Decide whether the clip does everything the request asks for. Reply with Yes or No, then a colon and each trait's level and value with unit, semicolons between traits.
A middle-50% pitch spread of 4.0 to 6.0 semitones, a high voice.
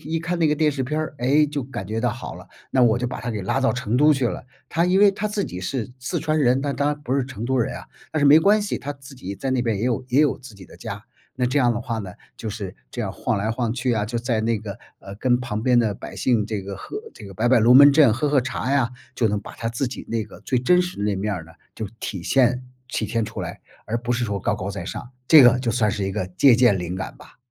No: average, 4.3 semitones; low, 120 Hz